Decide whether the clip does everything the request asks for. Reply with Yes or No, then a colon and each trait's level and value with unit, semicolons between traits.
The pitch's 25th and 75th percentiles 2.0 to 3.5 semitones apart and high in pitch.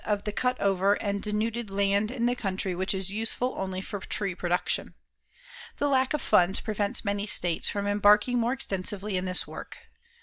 Yes: average, 2.8 semitones; high, 205 Hz